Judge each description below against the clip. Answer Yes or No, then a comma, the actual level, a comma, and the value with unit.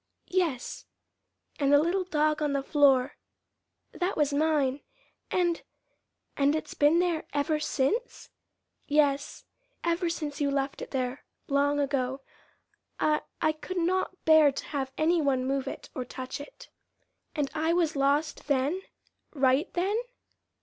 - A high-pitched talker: Yes, very high, 295 Hz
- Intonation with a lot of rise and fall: No, average, 3.0 semitones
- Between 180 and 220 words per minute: No, average, 140 wpm